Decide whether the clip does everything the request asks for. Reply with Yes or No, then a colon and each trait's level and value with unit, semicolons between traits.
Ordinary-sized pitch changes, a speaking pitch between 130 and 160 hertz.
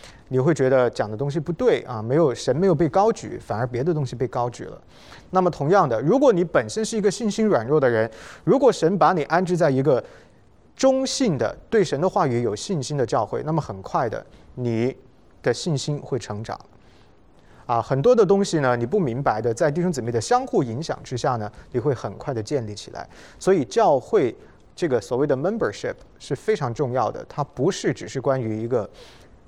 No: wide, 7.1 semitones; medium, 140 Hz